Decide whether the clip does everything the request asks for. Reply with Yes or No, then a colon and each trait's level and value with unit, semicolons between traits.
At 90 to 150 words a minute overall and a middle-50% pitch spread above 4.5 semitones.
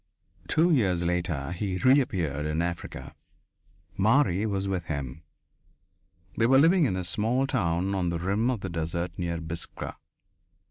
Yes: average, 145 wpm; average, 4.9 semitones